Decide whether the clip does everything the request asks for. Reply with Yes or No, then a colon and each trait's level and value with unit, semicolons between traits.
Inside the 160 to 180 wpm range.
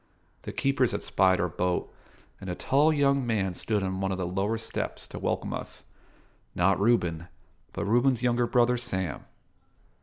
Yes: average, 170 wpm